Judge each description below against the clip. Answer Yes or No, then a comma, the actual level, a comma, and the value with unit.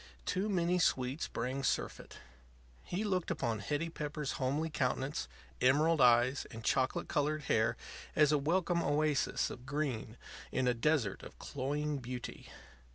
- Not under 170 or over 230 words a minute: No, average, 140 wpm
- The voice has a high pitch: No, medium, 145 Hz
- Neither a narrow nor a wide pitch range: Yes, average, 3.4 semitones